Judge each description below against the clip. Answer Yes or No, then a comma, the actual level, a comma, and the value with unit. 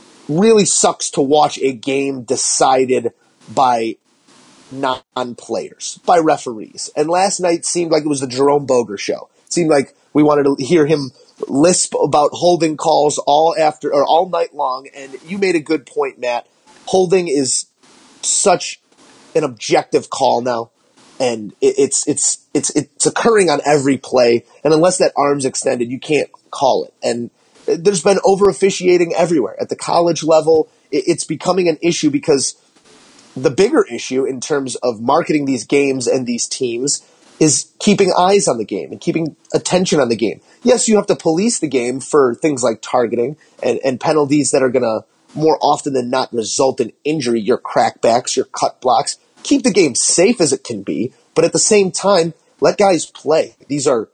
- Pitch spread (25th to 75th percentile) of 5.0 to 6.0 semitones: Yes, average, 5.3 semitones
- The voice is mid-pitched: Yes, medium, 160 Hz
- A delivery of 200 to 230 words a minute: No, average, 175 wpm